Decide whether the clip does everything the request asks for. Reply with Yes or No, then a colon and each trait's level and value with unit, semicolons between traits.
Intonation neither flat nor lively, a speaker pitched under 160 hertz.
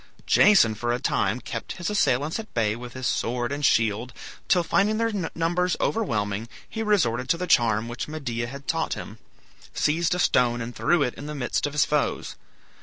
No: wide, 6.5 semitones; low, 135 Hz